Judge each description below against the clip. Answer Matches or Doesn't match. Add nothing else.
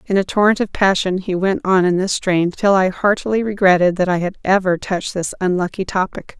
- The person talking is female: Matches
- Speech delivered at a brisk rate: Matches